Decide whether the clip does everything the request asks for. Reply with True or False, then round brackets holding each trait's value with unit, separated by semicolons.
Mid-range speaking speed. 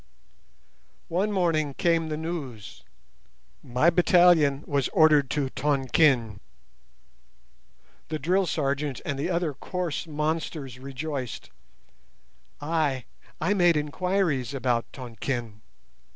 False (95 wpm)